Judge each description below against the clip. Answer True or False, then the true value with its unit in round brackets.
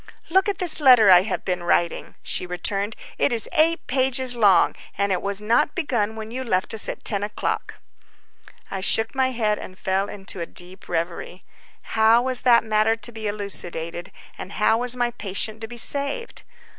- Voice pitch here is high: True (220 Hz)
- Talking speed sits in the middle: True (185 wpm)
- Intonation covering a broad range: False (4.2 semitones)